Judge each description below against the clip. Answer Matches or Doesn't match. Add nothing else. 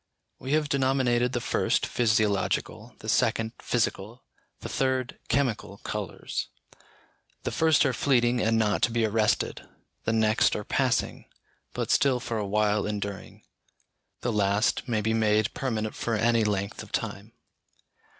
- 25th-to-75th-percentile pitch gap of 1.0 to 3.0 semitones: Matches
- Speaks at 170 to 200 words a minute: Doesn't match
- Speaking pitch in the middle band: Doesn't match